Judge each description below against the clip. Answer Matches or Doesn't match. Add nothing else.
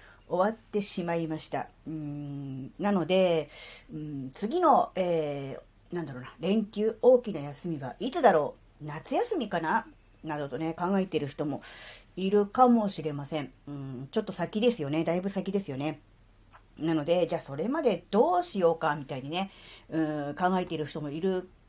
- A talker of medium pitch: Matches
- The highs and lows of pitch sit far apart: Doesn't match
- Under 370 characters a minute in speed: Matches